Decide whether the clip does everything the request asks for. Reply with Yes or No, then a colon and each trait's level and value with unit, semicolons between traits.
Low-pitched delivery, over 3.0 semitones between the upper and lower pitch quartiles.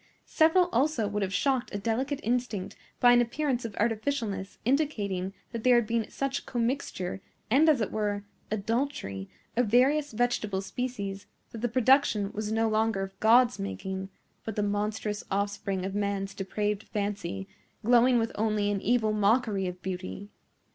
No: high, 215 Hz; average, 3.6 semitones